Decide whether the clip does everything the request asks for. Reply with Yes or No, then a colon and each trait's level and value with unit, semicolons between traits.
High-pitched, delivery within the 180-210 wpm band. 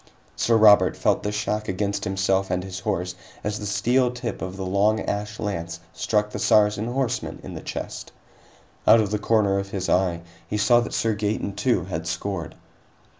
No: low, 105 Hz; average, 185 wpm